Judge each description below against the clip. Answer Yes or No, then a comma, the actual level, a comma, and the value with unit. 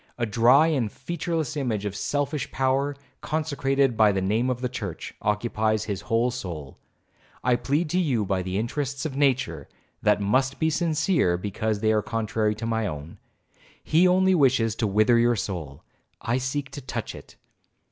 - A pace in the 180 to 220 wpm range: No, average, 165 wpm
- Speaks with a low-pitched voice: Yes, low, 120 Hz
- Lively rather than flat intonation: No, average, 4.9 semitones